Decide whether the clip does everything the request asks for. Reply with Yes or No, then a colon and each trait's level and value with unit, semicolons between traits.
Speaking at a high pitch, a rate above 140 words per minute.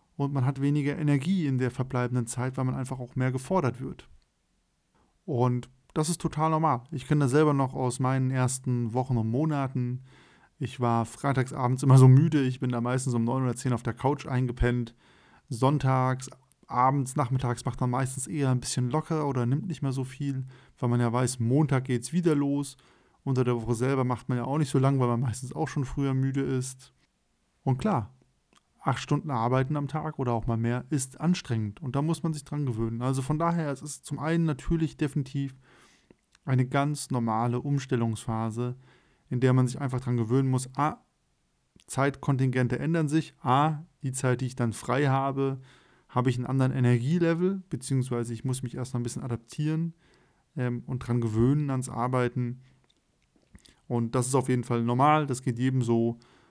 No: low, 130 Hz; fast, 190 wpm